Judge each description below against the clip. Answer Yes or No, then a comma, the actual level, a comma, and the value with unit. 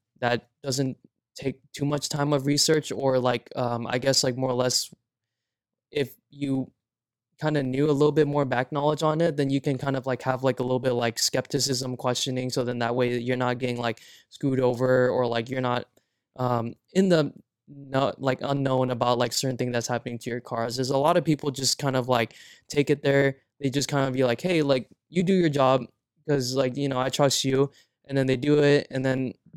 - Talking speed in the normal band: No, fast, 225 wpm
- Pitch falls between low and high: No, low, 130 Hz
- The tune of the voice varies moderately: No, narrow, 2.3 semitones